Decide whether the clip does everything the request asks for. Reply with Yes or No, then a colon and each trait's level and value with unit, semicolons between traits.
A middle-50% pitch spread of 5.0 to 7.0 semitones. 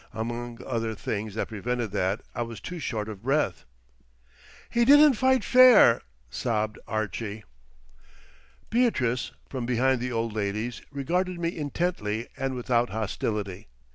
Yes: average, 5.3 semitones